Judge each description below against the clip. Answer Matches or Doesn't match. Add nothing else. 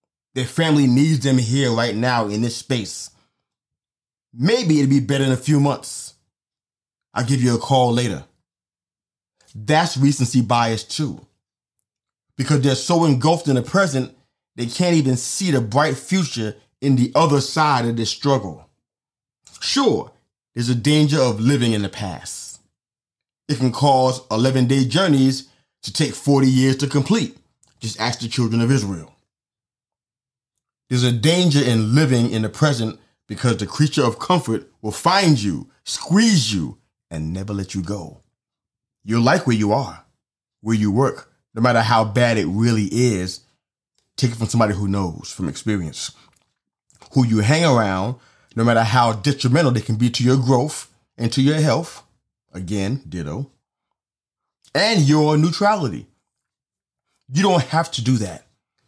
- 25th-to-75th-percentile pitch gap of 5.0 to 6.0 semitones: Doesn't match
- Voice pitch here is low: Matches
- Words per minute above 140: Matches